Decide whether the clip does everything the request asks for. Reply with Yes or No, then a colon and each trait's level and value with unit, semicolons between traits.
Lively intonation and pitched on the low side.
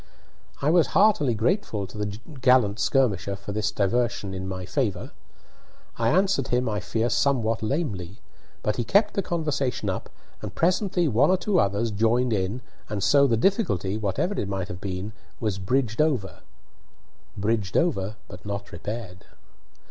Yes: wide, 5.8 semitones; low, 110 Hz